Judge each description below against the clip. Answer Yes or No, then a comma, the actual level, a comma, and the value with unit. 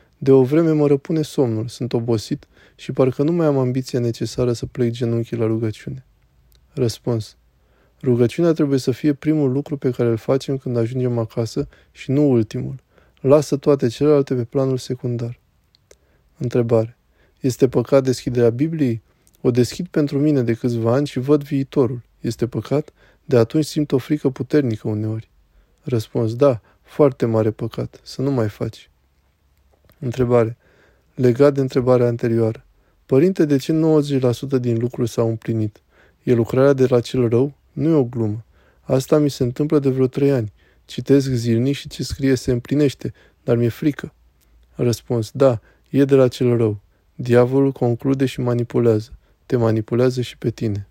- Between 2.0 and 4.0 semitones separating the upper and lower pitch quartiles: Yes, average, 3.3 semitones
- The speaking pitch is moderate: No, low, 125 Hz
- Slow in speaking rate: No, average, 155 wpm